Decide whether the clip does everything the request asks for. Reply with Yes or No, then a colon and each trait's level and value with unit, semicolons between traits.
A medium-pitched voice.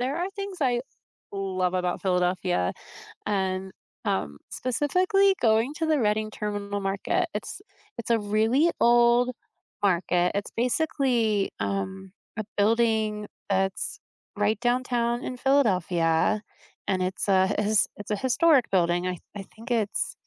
No: high, 210 Hz